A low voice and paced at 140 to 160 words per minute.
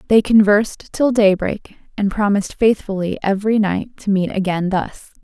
No: high, 205 Hz; average, 150 wpm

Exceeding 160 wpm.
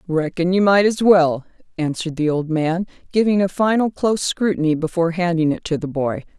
Yes: average, 190 wpm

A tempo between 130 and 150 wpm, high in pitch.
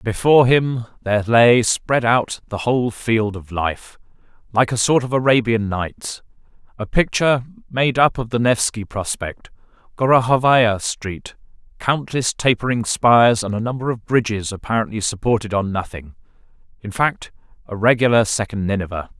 No: slow, 135 wpm; low, 115 Hz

